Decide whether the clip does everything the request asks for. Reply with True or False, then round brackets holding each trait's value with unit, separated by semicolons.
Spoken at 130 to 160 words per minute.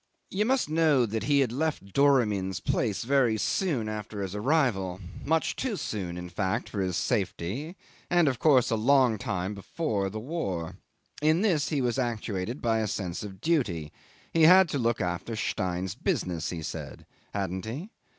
False (170 wpm)